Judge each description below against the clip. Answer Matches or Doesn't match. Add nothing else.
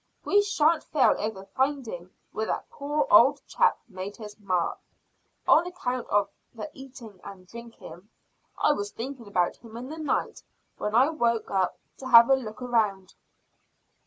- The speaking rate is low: Doesn't match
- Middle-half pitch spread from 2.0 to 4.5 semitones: Doesn't match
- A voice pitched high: Matches